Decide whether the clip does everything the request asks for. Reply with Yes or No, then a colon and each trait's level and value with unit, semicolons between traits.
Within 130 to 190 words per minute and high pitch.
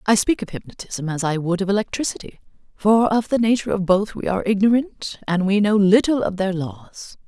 No: fast, 205 wpm; high, 200 Hz